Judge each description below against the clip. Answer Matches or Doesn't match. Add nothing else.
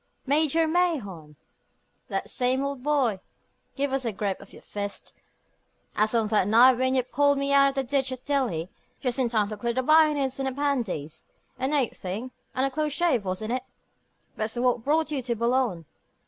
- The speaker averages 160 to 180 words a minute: Doesn't match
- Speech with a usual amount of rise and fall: Matches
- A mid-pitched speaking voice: Doesn't match